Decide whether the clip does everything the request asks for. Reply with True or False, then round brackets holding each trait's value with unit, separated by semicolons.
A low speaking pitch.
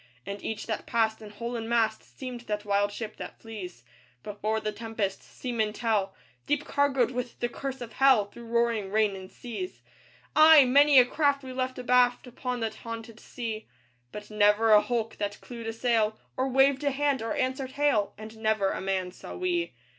False (230 Hz)